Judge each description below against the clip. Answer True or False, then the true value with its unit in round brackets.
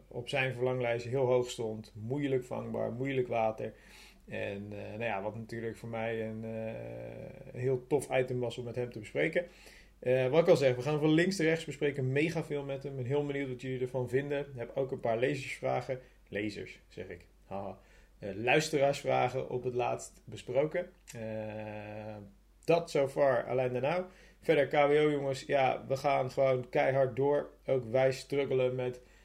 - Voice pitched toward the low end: True (130 Hz)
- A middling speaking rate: True (185 wpm)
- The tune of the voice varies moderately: True (3.8 semitones)